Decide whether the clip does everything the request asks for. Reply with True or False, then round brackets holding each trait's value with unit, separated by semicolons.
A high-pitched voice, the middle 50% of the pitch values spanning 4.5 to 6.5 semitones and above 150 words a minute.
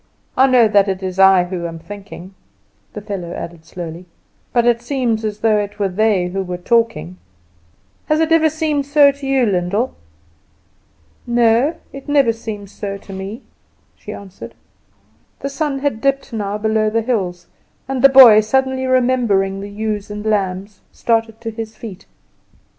True (215 Hz; 4.8 semitones; 165 wpm)